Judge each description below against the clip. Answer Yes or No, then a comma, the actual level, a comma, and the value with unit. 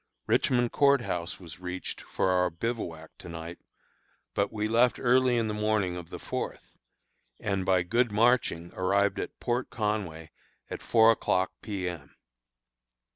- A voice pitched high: No, low, 100 Hz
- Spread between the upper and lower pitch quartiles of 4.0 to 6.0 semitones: Yes, average, 4.6 semitones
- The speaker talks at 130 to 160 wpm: Yes, average, 150 wpm